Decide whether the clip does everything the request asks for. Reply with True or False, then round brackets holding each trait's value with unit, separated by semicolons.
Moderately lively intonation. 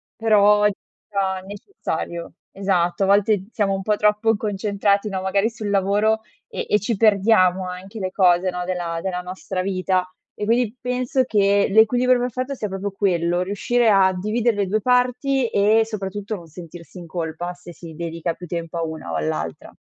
True (3.2 semitones)